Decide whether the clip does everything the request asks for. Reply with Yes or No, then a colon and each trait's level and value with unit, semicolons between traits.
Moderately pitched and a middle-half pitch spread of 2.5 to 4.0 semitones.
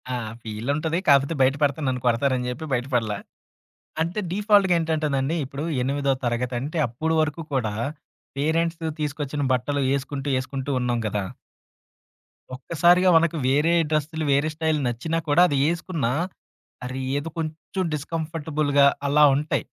Yes: medium, 145 Hz; average, 3.6 semitones